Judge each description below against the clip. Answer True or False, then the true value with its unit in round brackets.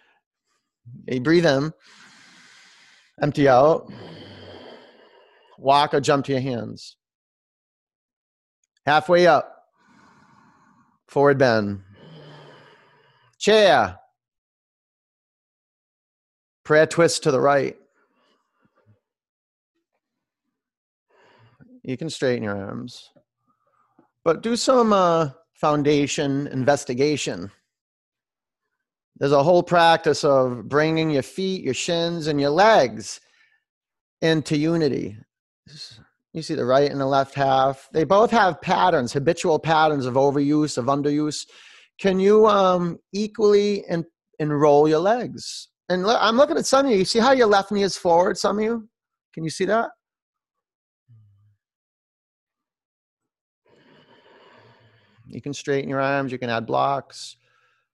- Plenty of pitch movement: True (6.0 semitones)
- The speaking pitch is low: False (150 Hz)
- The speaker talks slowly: True (110 wpm)